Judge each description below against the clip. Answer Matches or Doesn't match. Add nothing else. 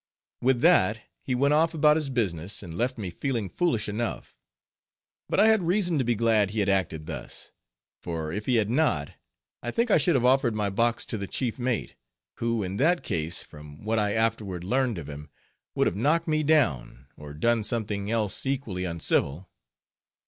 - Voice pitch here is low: Matches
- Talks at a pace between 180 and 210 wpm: Matches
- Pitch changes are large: Matches